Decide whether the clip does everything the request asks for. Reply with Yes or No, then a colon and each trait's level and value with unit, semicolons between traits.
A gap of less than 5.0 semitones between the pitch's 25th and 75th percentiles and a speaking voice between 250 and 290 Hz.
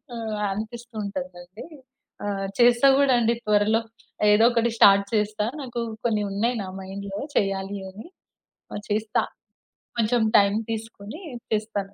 No: narrow, 2.5 semitones; high, 210 Hz